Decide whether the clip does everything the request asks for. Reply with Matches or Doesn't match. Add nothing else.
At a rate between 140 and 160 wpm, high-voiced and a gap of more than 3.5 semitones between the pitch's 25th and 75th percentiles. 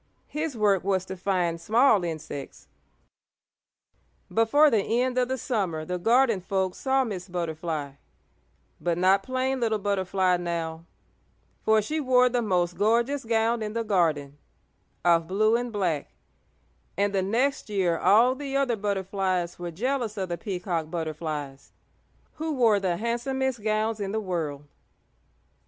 Matches